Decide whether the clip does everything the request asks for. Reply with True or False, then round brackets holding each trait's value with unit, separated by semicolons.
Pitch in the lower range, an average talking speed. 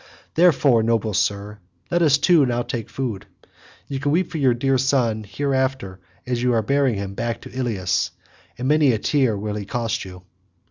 True (120 Hz; 180 wpm)